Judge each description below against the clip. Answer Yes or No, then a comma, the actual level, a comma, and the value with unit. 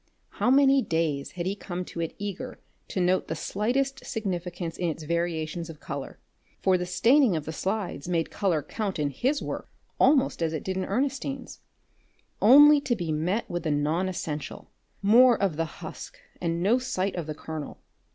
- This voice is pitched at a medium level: Yes, medium, 180 Hz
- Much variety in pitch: Yes, wide, 5.7 semitones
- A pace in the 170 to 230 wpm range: Yes, average, 180 wpm